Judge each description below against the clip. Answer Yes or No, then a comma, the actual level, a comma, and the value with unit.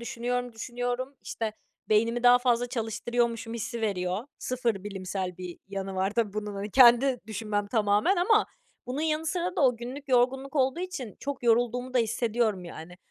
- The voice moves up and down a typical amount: Yes, average, 3.4 semitones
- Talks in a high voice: Yes, high, 235 Hz